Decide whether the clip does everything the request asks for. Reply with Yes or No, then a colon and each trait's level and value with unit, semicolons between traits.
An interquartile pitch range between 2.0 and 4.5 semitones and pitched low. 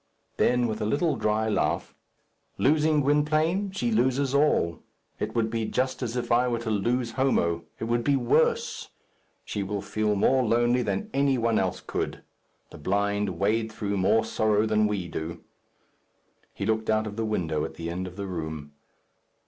Yes: average, 4.1 semitones; low, 110 Hz